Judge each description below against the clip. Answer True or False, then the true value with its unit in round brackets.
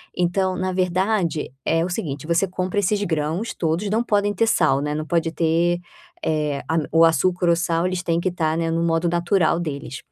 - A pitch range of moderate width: False (2.3 semitones)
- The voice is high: False (170 Hz)